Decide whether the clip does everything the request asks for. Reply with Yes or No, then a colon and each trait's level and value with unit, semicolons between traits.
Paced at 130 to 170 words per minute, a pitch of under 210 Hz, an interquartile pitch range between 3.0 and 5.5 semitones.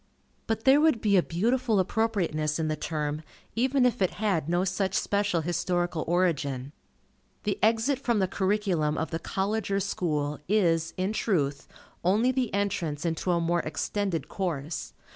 Yes: average, 160 wpm; medium, 185 Hz; average, 4.6 semitones